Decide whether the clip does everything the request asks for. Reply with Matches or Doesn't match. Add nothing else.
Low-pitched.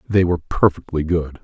Matches